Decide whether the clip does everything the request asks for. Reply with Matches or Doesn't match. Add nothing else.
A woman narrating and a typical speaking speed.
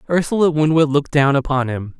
Doesn't match